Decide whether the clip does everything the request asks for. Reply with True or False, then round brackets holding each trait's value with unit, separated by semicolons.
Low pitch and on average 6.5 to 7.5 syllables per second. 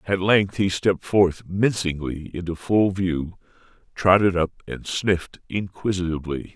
False (95 Hz; 4.5 syllables/s)